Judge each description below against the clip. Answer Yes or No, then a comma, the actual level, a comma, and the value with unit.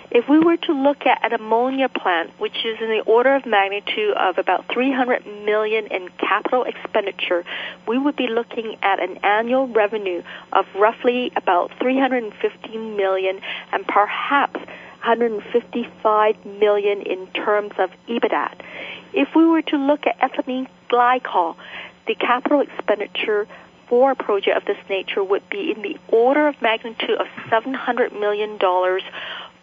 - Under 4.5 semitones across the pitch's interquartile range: No, average, 4.8 semitones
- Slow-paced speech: No, average, 145 wpm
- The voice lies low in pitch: No, high, 235 Hz